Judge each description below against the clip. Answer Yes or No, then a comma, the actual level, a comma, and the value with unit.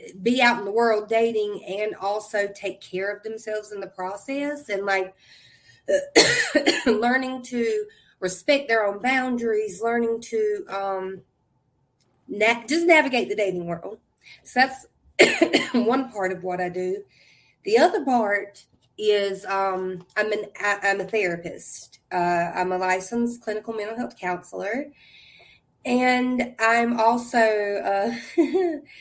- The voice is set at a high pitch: Yes, high, 215 Hz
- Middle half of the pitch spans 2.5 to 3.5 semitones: No, average, 4.7 semitones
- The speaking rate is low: Yes, slow, 130 wpm